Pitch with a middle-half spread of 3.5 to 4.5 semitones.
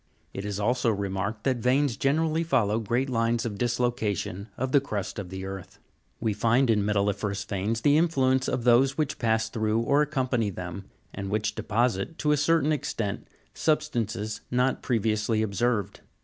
Yes: average, 4.2 semitones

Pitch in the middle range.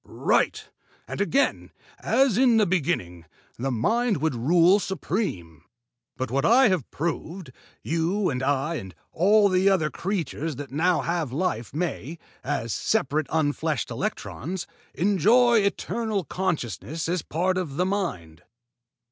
Yes: medium, 170 Hz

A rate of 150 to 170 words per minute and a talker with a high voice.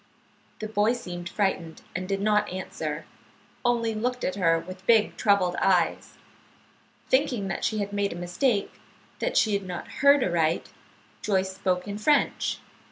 Yes: average, 160 wpm; high, 200 Hz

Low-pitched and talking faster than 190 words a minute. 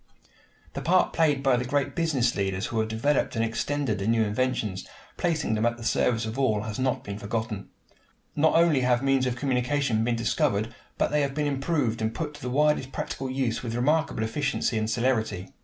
Yes: low, 125 Hz; average, 200 wpm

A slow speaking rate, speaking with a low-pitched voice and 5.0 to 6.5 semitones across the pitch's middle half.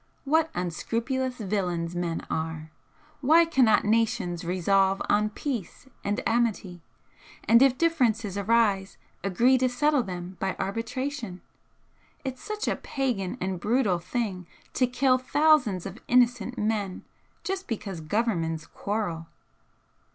No: slow, 120 wpm; high, 215 Hz; wide, 5.6 semitones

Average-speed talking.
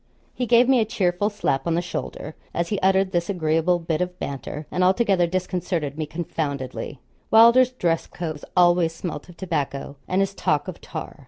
Yes: average, 180 wpm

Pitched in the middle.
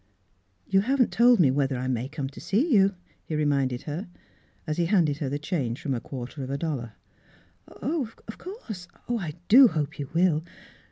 Yes: medium, 155 Hz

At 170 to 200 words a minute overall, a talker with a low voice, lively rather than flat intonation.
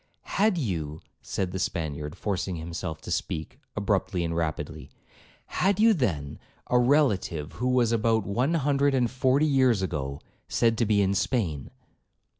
No: average, 150 wpm; low, 105 Hz; wide, 7.6 semitones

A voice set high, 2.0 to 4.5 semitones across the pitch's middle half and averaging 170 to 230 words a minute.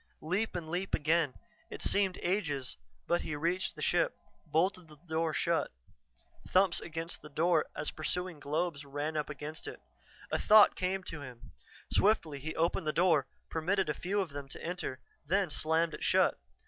No: medium, 165 Hz; average, 3.3 semitones; average, 175 wpm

